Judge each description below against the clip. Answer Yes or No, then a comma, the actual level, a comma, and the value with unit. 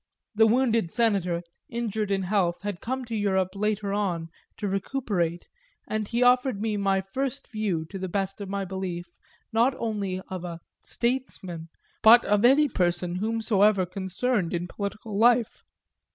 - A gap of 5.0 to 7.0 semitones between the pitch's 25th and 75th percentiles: No, average, 3.5 semitones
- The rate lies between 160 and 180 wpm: No, average, 150 wpm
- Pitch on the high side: Yes, high, 200 Hz